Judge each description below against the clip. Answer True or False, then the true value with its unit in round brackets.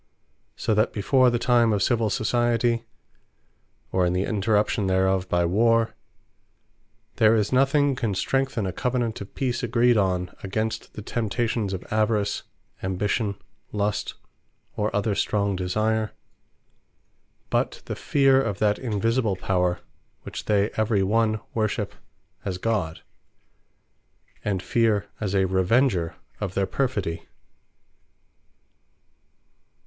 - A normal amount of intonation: True (3.2 semitones)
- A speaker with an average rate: False (120 wpm)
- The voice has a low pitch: True (105 Hz)